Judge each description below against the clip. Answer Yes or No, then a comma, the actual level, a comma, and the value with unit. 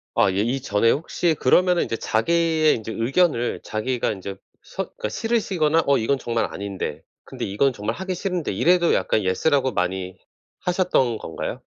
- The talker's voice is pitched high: No, low, 125 Hz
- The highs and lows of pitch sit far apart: Yes, wide, 8.0 semitones